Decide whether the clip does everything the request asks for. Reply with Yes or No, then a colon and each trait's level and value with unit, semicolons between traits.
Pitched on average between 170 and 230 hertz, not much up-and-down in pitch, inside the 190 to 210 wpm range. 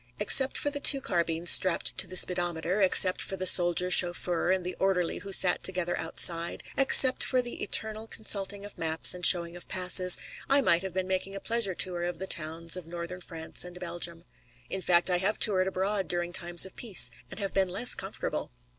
Yes: medium, 185 Hz; narrow, 2.0 semitones; average, 200 wpm